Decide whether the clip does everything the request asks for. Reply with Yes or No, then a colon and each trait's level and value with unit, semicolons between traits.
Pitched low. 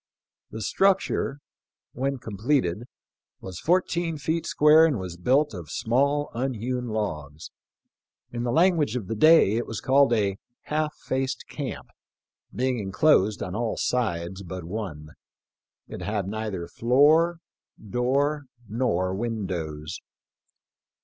Yes: low, 120 Hz